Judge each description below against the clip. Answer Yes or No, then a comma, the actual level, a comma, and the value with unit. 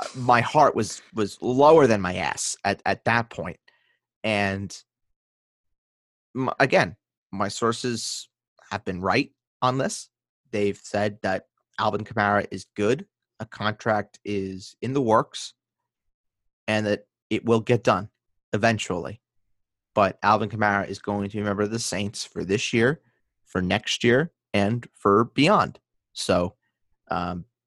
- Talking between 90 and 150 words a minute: Yes, average, 140 wpm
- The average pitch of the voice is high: No, low, 105 Hz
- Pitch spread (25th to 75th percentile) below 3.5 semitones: Yes, average, 2.8 semitones